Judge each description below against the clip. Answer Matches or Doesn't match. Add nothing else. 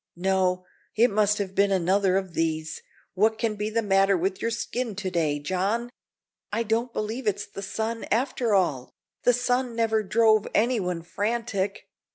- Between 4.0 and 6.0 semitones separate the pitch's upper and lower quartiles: Doesn't match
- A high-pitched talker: Matches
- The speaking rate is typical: Matches